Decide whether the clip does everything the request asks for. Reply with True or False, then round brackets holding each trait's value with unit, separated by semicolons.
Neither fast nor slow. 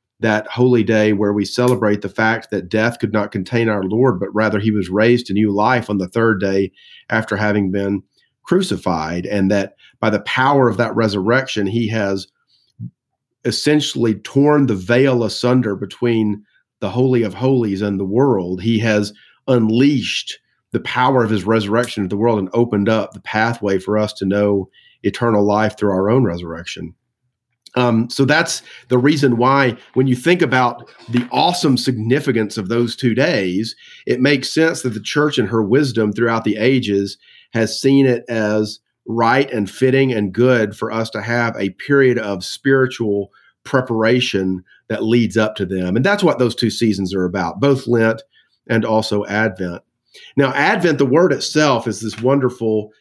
True (175 wpm)